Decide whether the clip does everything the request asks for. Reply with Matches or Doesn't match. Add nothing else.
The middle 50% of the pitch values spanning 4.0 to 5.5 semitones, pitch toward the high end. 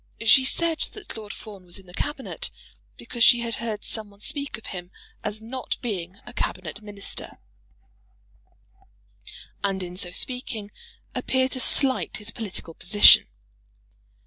Matches